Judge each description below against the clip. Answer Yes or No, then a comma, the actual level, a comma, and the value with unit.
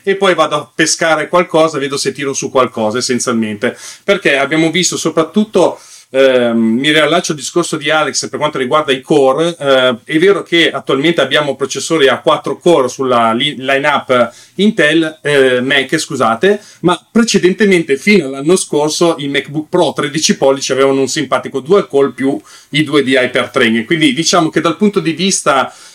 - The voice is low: No, medium, 150 Hz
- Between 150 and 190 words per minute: Yes, average, 165 wpm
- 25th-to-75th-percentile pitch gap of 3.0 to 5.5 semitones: Yes, average, 4.3 semitones